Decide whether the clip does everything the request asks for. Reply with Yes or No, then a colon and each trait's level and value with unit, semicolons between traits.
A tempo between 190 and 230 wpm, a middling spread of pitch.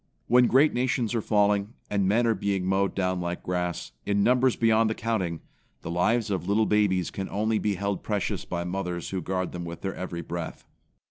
Yes: average, 200 wpm; average, 3.5 semitones